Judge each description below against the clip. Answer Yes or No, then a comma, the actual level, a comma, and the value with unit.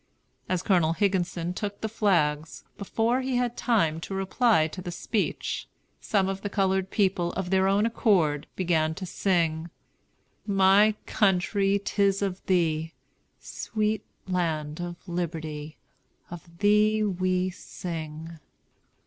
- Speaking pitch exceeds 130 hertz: Yes, medium, 185 Hz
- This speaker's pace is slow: Yes, slow, 125 wpm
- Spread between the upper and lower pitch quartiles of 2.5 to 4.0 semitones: Yes, average, 3.4 semitones